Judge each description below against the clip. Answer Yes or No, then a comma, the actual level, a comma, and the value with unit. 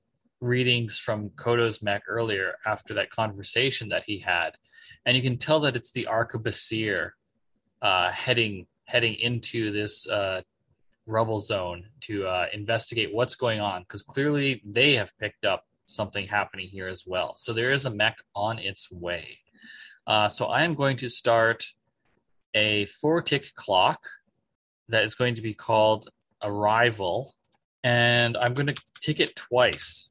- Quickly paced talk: No, average, 155 wpm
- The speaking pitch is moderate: No, low, 115 Hz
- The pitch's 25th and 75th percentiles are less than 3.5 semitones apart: Yes, average, 3.0 semitones